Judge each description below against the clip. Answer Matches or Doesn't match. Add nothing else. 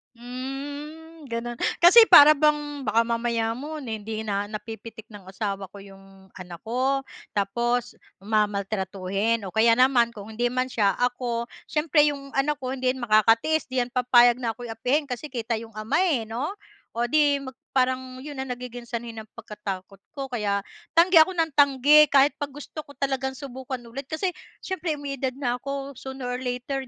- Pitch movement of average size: Matches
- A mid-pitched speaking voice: Doesn't match